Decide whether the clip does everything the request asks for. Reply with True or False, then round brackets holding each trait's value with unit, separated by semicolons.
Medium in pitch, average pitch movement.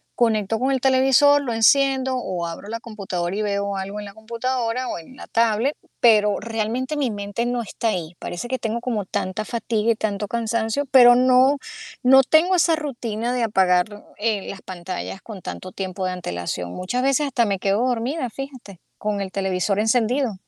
False (225 Hz; 4.1 semitones)